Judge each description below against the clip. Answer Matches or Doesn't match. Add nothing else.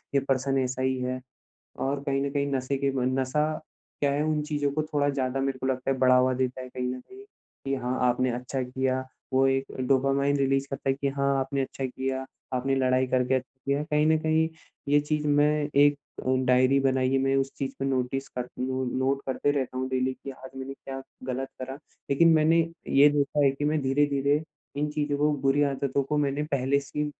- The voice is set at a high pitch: Doesn't match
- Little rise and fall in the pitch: Matches